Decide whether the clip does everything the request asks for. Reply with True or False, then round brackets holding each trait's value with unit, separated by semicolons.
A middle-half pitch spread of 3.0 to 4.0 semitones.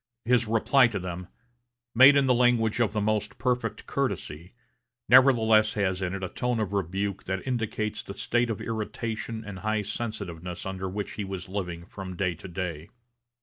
True (3.6 semitones)